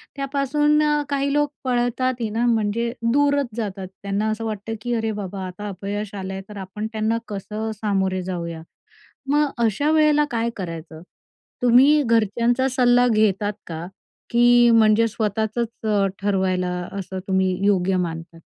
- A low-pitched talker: No, high, 220 Hz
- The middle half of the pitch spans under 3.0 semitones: No, average, 4.1 semitones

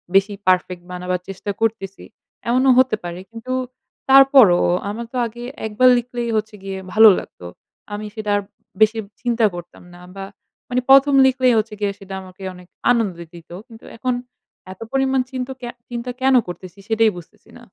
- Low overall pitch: No, high, 220 Hz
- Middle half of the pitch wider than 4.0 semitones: Yes, average, 4.5 semitones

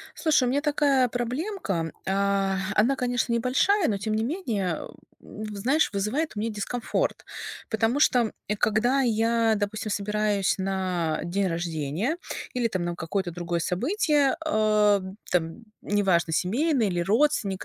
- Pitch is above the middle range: Yes, high, 215 Hz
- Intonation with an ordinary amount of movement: Yes, average, 4.7 semitones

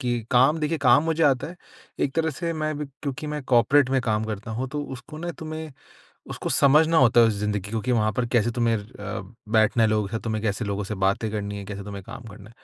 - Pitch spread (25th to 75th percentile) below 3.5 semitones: No, wide, 5.5 semitones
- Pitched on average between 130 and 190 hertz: No, low, 120 Hz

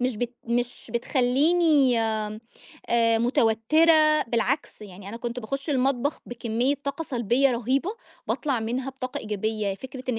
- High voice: Yes, high, 245 Hz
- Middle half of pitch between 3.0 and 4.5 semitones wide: Yes, average, 3.5 semitones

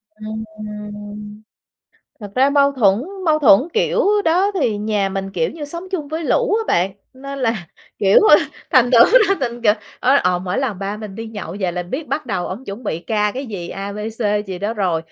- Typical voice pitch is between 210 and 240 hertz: Yes, high, 215 Hz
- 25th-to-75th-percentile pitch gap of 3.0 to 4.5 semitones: No, average, 5.1 semitones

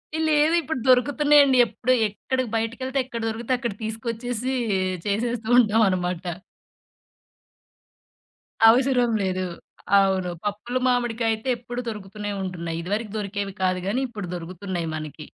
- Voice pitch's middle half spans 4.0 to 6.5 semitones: Yes, average, 4.3 semitones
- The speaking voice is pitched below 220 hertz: No, high, 225 Hz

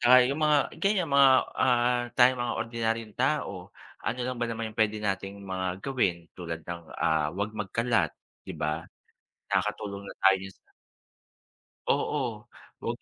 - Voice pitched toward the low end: Yes, low, 110 Hz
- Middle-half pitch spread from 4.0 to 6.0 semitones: Yes, average, 4.4 semitones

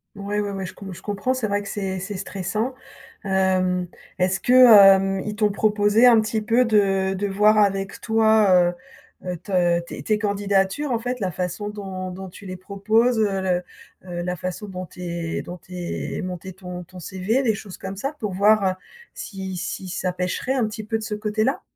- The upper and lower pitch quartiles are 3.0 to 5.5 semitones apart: No, narrow, 2.6 semitones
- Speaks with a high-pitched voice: Yes, high, 195 Hz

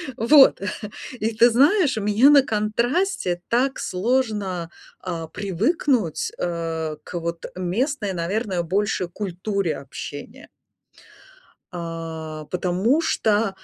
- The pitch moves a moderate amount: No, wide, 5.9 semitones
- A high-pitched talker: Yes, high, 200 Hz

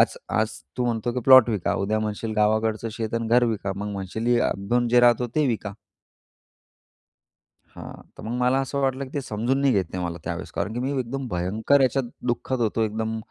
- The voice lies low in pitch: Yes, low, 115 Hz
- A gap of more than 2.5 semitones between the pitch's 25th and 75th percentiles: Yes, average, 2.9 semitones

